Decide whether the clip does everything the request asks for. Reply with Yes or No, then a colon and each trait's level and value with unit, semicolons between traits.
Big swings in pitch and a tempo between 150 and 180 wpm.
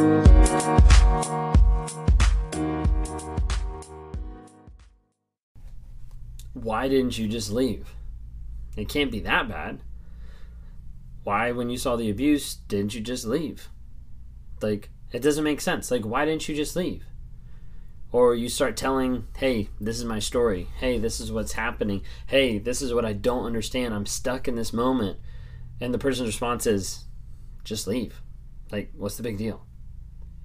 No: wide, 7.8 semitones; slow, 135 wpm